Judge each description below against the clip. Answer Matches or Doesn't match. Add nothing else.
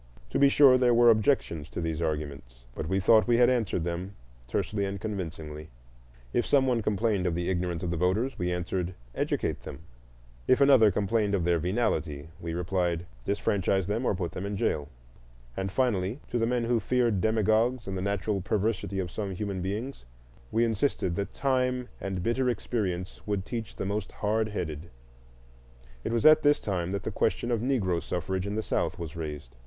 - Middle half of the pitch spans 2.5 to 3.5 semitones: Doesn't match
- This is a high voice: Doesn't match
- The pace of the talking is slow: Doesn't match